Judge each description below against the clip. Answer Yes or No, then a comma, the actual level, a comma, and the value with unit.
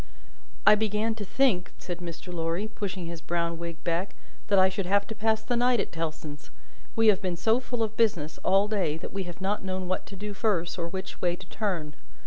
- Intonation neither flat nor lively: Yes, average, 3.8 semitones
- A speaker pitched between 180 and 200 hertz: Yes, high, 190 Hz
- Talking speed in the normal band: No, fast, 220 wpm